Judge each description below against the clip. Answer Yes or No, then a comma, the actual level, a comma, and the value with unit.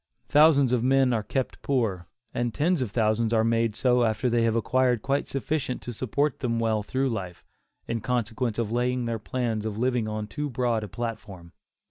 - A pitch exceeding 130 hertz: No, low, 120 Hz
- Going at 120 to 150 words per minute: No, average, 190 wpm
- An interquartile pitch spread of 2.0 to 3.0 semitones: Yes, average, 2.7 semitones